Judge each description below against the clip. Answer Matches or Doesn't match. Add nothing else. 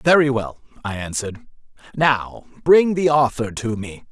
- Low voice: Matches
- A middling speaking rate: Matches